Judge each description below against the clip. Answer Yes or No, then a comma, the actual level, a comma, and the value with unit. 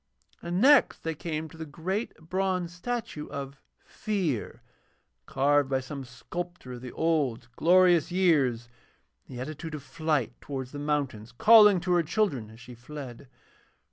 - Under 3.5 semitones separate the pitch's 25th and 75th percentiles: No, average, 5.1 semitones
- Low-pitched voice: No, medium, 150 Hz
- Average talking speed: Yes, average, 150 wpm